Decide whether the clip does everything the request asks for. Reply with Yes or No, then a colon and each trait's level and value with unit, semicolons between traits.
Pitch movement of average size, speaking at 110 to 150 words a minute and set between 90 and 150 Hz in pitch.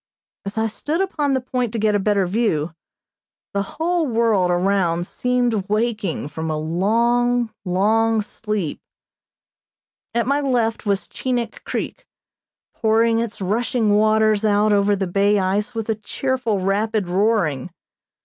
No: average, 3.0 semitones; average, 140 wpm; high, 215 Hz